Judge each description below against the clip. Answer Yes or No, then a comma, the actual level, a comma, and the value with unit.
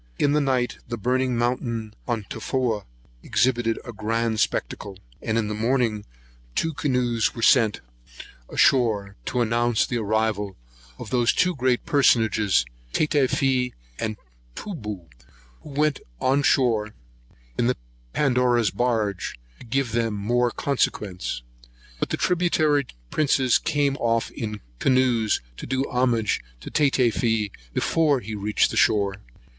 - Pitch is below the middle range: Yes, low, 120 Hz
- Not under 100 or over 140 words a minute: Yes, slow, 135 wpm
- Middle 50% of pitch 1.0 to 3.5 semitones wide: Yes, average, 3.2 semitones